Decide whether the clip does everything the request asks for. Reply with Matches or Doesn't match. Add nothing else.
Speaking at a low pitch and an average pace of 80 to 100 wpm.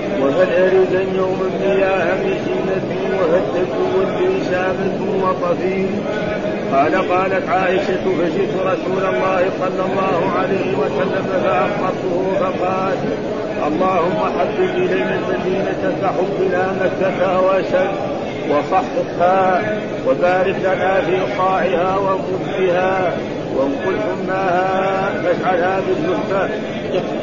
Doesn't match